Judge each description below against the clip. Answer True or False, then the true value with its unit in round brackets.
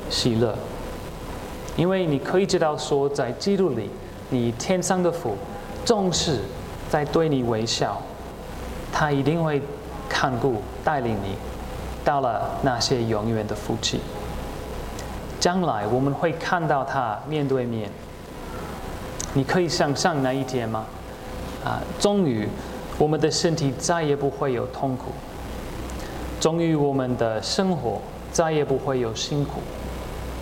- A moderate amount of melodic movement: False (6.0 semitones)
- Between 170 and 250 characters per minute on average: True (185 characters per minute)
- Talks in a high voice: False (135 Hz)